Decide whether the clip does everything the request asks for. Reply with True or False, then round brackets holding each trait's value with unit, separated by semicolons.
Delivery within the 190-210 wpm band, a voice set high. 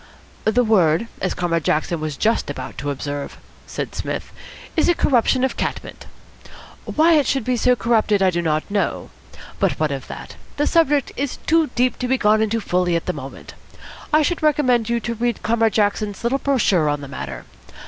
True (195 wpm; 220 Hz)